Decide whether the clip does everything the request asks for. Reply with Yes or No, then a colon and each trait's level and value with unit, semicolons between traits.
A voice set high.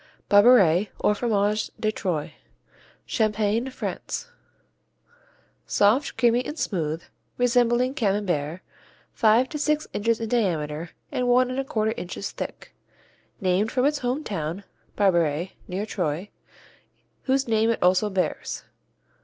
Yes: high, 215 Hz